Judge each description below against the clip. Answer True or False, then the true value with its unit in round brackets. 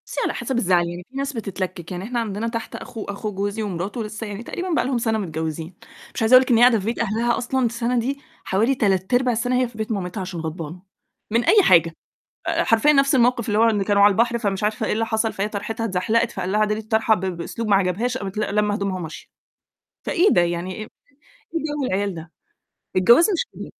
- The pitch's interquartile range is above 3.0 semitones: True (3.8 semitones)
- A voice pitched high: True (215 Hz)